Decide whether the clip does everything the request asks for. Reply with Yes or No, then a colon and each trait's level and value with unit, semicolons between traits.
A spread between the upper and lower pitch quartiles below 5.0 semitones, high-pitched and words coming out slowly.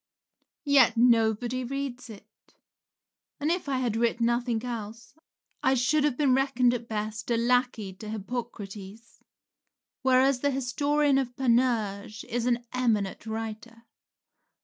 Yes: average, 2.7 semitones; high, 240 Hz; slow, 125 wpm